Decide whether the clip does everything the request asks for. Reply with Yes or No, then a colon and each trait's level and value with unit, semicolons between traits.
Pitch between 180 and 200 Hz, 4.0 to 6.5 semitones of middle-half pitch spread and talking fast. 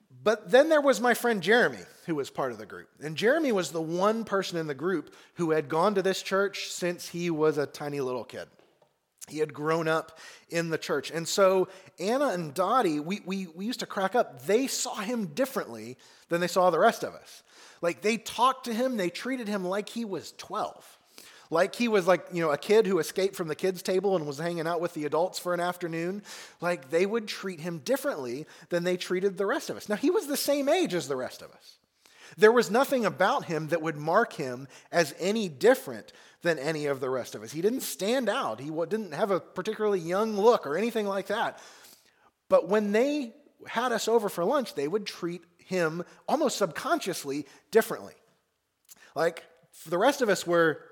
Yes: high, 190 Hz; average, 4.9 semitones; fast, 210 wpm